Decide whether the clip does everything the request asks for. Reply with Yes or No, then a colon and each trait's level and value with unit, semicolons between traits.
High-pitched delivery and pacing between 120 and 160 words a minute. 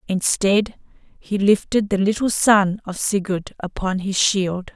Yes: high, 195 Hz; average, 140 wpm